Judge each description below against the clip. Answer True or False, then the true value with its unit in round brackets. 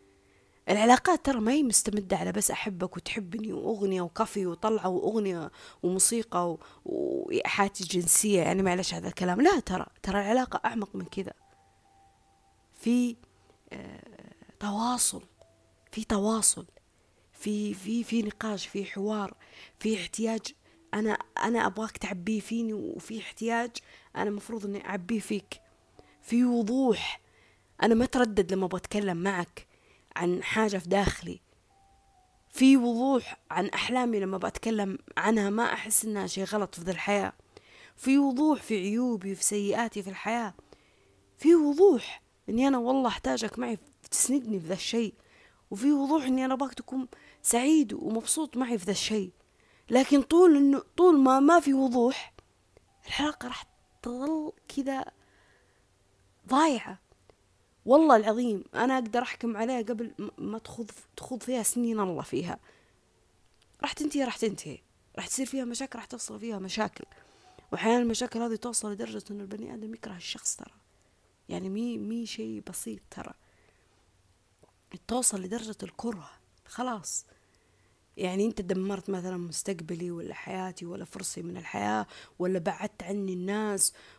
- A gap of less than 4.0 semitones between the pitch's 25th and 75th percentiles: False (4.7 semitones)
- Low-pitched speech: False (215 Hz)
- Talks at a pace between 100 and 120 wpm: False (135 wpm)